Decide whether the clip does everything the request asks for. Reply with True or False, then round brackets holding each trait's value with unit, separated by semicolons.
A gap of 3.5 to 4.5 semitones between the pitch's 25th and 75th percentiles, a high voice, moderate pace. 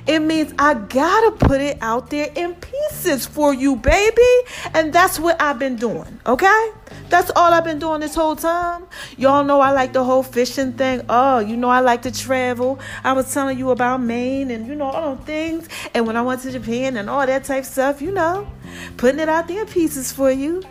False (4.0 semitones; 275 Hz; 220 wpm)